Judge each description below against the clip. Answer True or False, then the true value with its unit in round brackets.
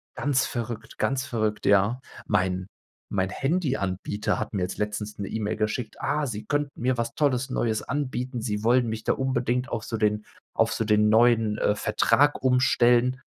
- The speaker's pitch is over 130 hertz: False (115 Hz)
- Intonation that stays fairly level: False (3.4 semitones)